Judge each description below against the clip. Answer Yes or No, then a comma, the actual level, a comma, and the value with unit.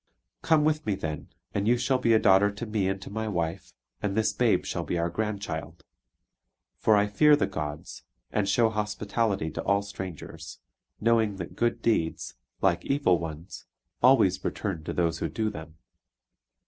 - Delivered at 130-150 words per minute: No, average, 175 wpm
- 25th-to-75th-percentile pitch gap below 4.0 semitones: No, average, 4.4 semitones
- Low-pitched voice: Yes, low, 100 Hz